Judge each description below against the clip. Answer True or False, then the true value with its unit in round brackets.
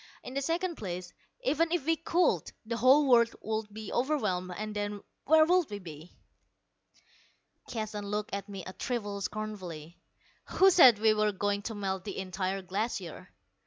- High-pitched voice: True (210 Hz)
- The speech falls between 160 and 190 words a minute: True (165 wpm)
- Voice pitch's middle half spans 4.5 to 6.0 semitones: True (4.9 semitones)